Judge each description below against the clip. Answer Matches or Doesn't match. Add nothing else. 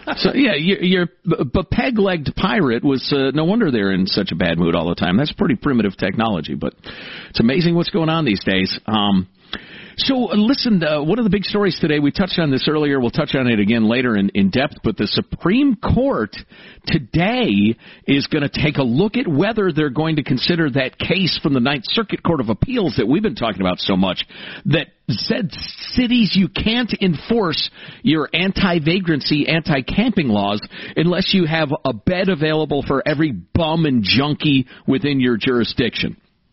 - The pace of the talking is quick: Doesn't match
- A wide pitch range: Matches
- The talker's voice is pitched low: Doesn't match